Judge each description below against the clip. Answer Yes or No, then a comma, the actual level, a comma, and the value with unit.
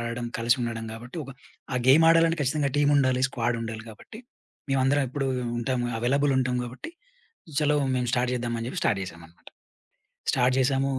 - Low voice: Yes, low, 125 Hz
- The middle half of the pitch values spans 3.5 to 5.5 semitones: No, average, 2.9 semitones